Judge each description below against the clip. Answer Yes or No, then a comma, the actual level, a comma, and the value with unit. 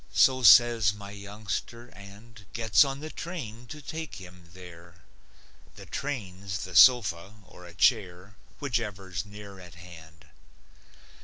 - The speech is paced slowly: Yes, slow, 130 wpm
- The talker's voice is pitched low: Yes, low, 100 Hz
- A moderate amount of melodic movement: Yes, average, 4.7 semitones